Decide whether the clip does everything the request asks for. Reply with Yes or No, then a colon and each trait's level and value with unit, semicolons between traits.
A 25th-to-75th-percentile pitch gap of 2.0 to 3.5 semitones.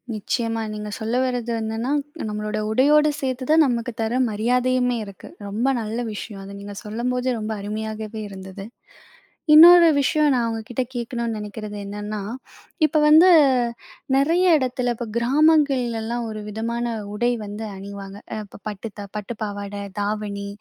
Yes: average, 3.2 semitones